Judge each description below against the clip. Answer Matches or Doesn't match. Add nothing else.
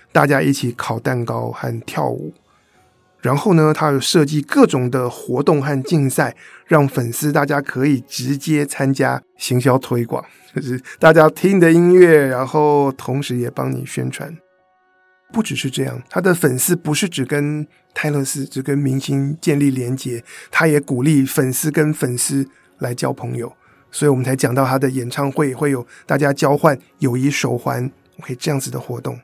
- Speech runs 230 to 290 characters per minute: Matches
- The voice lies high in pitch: Doesn't match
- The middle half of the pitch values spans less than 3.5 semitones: Matches